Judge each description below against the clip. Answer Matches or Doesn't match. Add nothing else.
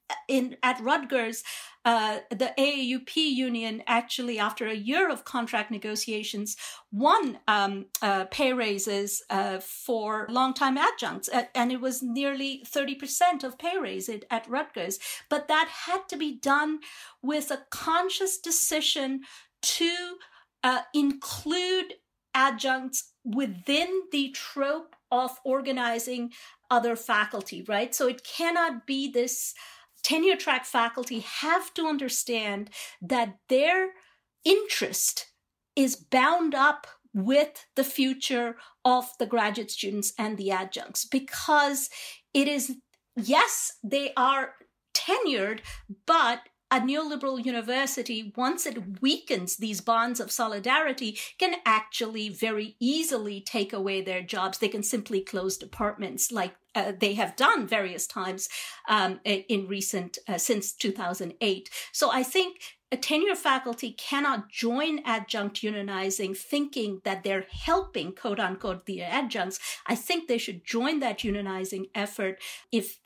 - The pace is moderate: Doesn't match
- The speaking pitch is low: Doesn't match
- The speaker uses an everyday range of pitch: Matches